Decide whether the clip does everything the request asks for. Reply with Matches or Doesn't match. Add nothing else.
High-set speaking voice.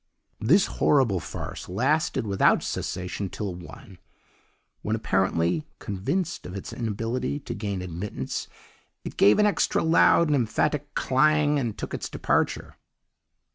Doesn't match